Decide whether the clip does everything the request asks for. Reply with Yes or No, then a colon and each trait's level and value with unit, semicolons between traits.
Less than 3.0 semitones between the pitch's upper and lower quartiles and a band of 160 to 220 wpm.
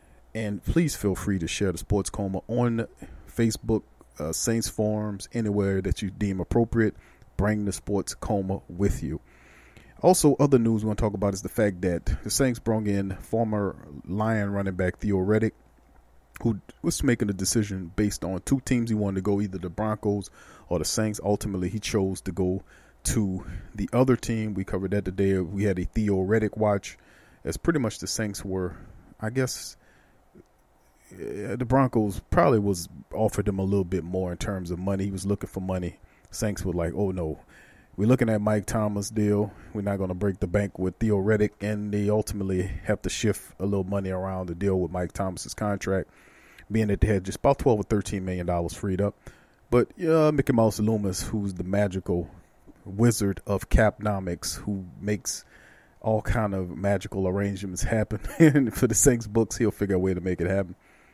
Yes: narrow, 2.5 semitones; average, 185 wpm